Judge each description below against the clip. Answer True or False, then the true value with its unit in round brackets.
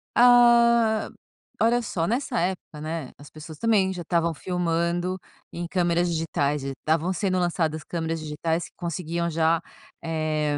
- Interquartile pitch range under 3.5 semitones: True (2.8 semitones)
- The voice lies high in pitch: False (170 Hz)